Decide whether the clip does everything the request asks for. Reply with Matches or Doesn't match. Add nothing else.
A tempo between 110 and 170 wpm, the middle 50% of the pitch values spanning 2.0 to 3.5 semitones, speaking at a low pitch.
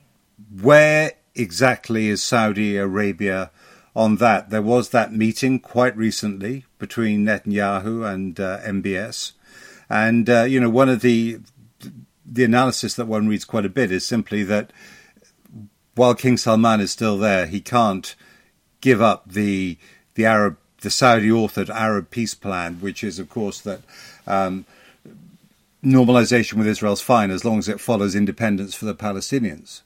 Matches